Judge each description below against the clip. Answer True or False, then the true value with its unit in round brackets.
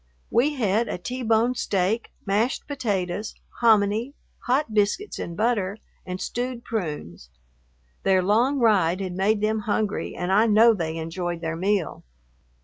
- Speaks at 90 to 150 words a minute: True (140 wpm)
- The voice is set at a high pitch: True (210 Hz)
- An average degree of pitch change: True (4.1 semitones)